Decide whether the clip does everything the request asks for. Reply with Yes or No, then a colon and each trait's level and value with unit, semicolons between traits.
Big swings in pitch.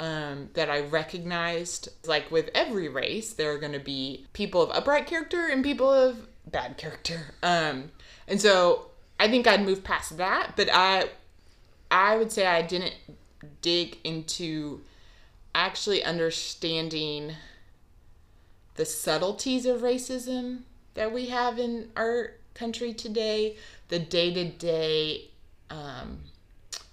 Yes: wide, 6.9 semitones